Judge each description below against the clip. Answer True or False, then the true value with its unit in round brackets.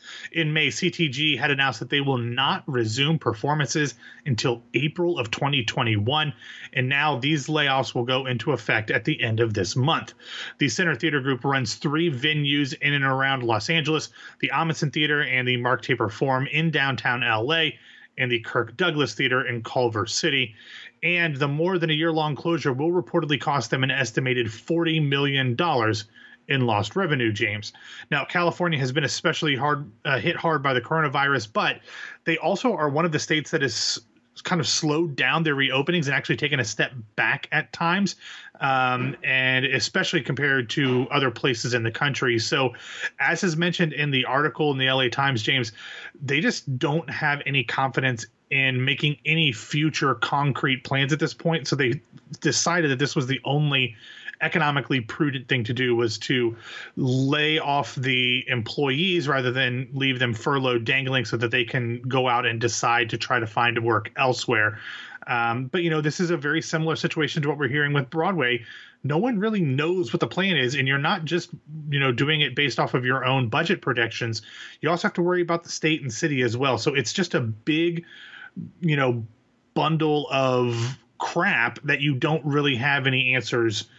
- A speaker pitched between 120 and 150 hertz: True (140 Hz)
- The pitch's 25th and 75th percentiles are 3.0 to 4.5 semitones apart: True (3.9 semitones)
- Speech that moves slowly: False (185 wpm)